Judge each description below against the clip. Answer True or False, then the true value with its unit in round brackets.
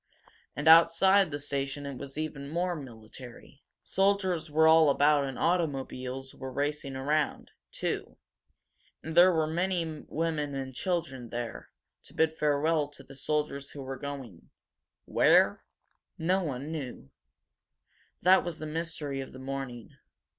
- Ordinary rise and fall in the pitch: True (3.2 semitones)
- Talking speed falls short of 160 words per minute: True (140 wpm)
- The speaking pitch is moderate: True (145 Hz)